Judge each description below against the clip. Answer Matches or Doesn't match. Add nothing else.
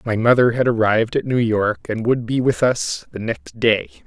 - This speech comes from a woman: Doesn't match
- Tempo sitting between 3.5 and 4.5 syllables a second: Doesn't match